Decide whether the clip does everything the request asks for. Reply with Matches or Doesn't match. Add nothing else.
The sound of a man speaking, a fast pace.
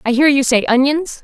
Doesn't match